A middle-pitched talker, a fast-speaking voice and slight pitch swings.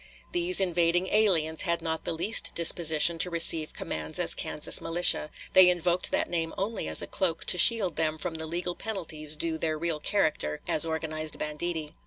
No: medium, 165 Hz; average, 180 wpm; narrow, 2.2 semitones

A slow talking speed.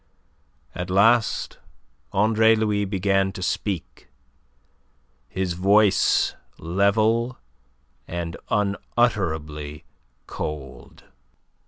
Yes: slow, 65 wpm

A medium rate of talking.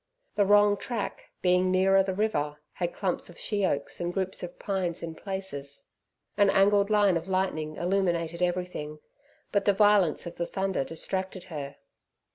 Yes: average, 155 wpm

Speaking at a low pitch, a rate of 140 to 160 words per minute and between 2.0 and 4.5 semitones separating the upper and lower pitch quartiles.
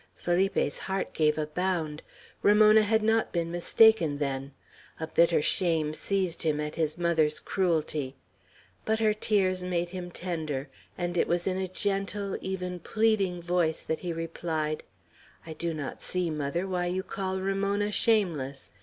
No: medium, 175 Hz; average, 155 wpm; average, 3.5 semitones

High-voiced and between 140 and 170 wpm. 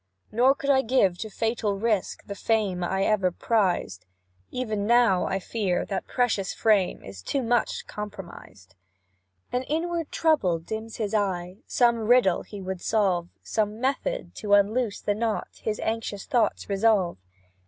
Yes: high, 215 Hz; average, 150 wpm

